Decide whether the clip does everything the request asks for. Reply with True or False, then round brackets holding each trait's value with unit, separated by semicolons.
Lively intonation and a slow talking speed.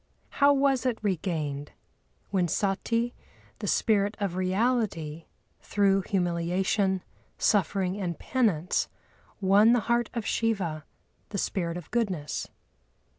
False (4.3 semitones; 110 wpm)